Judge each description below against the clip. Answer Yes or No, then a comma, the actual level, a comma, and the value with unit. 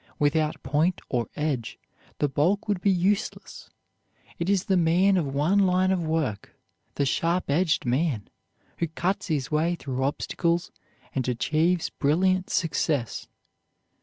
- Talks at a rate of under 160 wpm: Yes, slow, 135 wpm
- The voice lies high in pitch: No, medium, 165 Hz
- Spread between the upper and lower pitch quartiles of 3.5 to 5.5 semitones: Yes, average, 4.2 semitones